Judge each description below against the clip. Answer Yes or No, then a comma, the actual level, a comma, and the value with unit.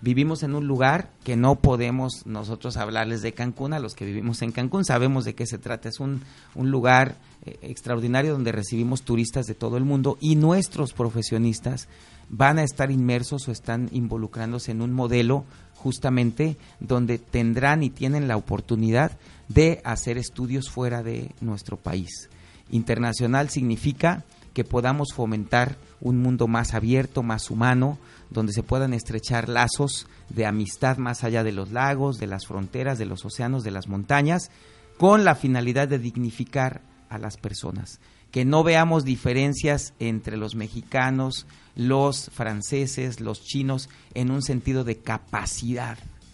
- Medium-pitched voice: No, low, 125 Hz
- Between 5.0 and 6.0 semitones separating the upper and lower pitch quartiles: No, average, 3.0 semitones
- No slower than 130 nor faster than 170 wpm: Yes, average, 155 wpm